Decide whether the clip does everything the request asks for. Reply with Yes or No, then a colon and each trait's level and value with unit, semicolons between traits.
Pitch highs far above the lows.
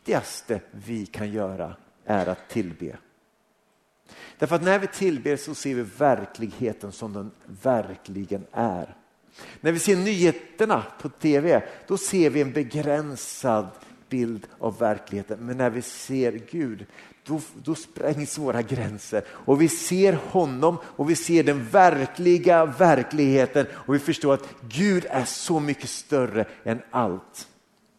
Yes: wide, 6.6 semitones